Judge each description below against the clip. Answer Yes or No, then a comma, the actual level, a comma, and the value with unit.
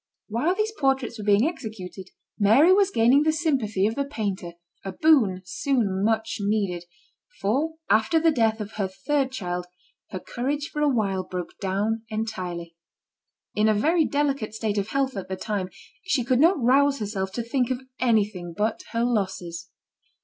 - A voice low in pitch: No, high, 220 Hz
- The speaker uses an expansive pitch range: Yes, wide, 5.8 semitones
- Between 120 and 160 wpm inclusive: No, average, 170 wpm